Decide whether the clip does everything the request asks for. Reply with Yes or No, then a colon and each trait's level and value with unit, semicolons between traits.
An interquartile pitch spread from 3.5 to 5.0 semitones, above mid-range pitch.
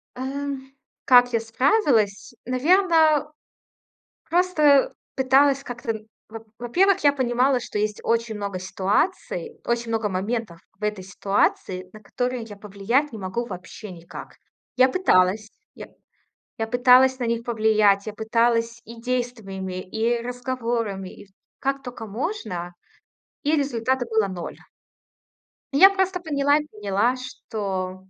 Yes: average, 4.2 semitones; high, 235 Hz